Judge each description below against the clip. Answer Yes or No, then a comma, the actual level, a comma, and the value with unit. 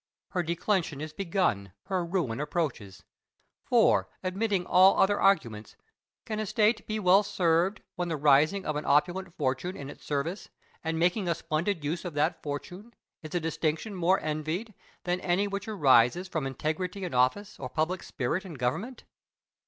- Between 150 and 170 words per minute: Yes, average, 165 wpm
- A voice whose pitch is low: No, medium, 170 Hz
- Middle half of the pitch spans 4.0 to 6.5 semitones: Yes, average, 4.3 semitones